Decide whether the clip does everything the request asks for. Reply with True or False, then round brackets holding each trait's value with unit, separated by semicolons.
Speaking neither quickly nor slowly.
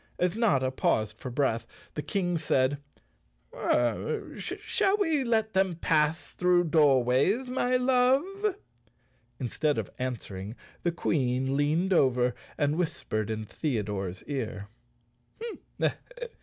False (115 wpm)